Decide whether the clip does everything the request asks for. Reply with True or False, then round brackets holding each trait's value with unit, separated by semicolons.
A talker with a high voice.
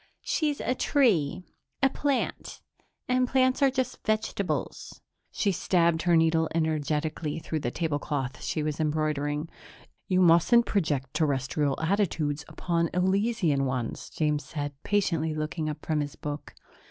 False (160 Hz)